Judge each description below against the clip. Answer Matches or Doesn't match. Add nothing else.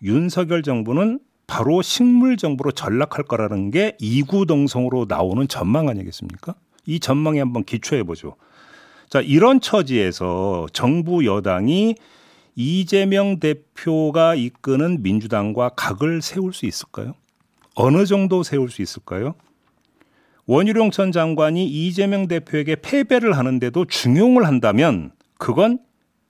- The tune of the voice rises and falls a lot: Matches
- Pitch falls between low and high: Matches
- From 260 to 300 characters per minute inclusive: Matches